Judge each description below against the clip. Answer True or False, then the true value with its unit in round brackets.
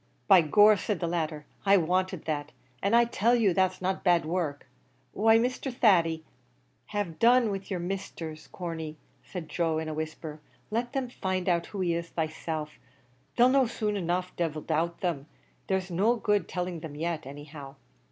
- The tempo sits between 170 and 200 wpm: True (180 wpm)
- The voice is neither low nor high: True (175 Hz)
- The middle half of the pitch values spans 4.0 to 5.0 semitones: True (4.3 semitones)